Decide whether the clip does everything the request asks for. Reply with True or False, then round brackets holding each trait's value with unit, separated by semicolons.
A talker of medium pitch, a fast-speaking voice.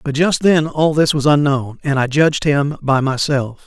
True (145 Hz; 215 wpm)